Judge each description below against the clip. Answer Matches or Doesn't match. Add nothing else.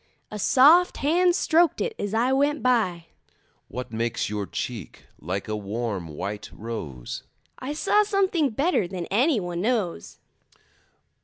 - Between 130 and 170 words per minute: Matches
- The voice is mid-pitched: Doesn't match